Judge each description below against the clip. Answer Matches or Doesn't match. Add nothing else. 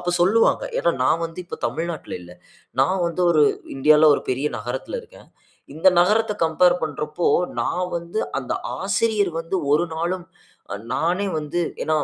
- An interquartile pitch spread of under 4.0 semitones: Matches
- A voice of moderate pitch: Matches